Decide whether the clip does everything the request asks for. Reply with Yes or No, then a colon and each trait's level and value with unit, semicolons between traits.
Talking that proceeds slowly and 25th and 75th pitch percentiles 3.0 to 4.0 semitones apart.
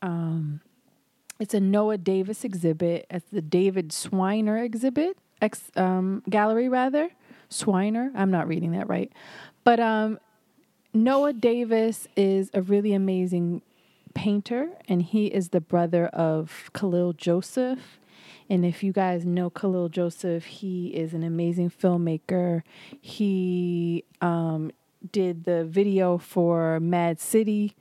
Yes: slow, 125 wpm; average, 3.6 semitones